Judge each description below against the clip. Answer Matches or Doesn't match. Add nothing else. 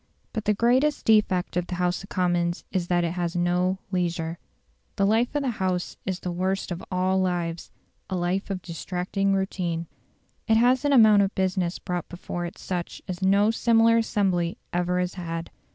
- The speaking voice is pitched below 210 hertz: Matches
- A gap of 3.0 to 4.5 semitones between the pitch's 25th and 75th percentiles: Doesn't match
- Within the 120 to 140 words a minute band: Doesn't match